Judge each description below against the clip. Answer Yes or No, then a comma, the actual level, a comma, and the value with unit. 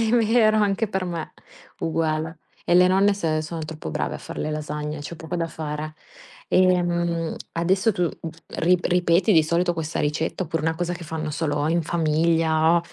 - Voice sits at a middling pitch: Yes, medium, 165 Hz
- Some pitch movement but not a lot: No, narrow, 2.3 semitones